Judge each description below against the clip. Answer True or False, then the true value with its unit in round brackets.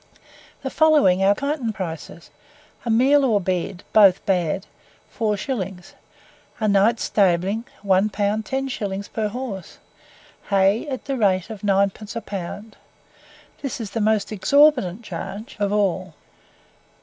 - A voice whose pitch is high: True (205 Hz)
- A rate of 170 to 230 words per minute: False (135 wpm)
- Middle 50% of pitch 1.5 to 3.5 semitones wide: True (3.2 semitones)